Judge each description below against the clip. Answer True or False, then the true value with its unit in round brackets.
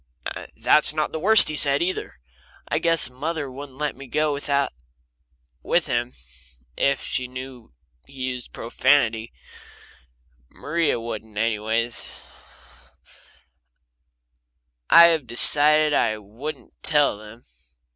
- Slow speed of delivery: True (110 wpm)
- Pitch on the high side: False (135 Hz)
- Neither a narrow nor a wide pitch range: True (4.5 semitones)